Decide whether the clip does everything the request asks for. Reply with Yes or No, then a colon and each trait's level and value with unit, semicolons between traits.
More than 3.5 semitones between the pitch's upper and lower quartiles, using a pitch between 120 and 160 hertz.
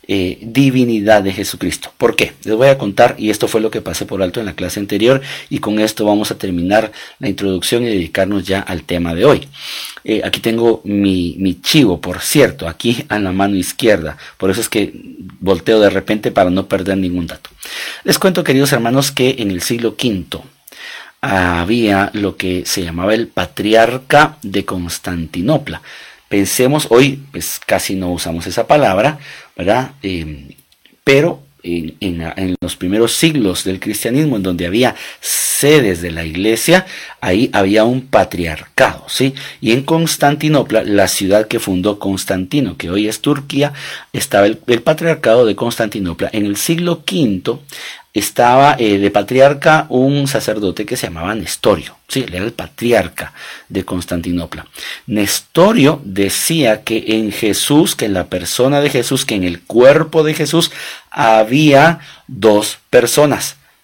No: average, 5.2 semitones; low, 105 Hz